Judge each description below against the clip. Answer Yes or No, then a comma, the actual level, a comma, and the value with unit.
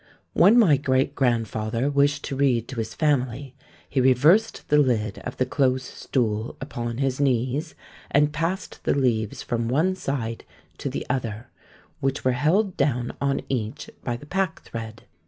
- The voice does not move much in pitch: No, average, 3.6 semitones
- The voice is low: Yes, low, 130 Hz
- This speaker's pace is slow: No, average, 155 wpm